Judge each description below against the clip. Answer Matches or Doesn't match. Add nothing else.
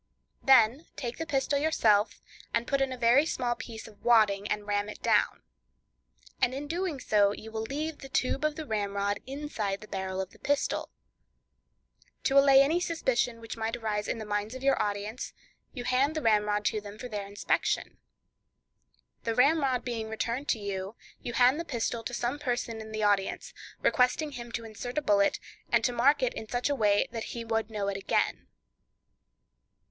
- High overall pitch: Matches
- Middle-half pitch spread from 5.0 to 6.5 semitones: Doesn't match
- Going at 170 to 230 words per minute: Matches